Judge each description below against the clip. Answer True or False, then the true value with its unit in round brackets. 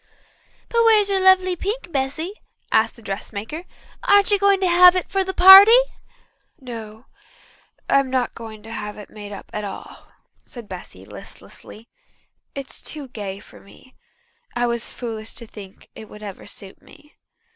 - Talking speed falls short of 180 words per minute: True (165 wpm)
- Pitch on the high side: True (255 Hz)